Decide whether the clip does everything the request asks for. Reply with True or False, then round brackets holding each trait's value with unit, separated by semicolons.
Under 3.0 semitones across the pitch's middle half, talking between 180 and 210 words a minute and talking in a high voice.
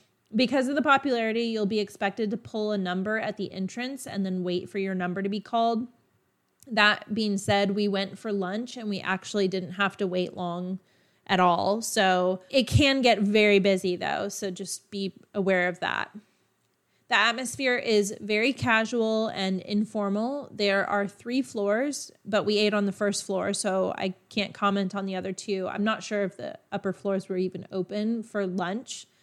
True (2.4 semitones; 185 wpm; 205 Hz)